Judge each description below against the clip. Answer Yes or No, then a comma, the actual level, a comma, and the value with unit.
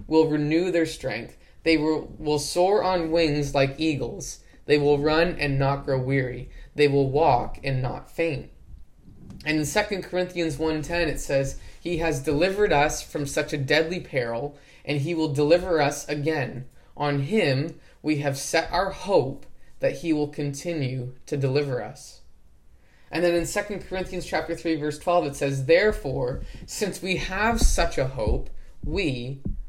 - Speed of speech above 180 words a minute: No, average, 160 wpm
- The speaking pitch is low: No, medium, 150 Hz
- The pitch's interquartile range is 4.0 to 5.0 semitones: No, average, 3.2 semitones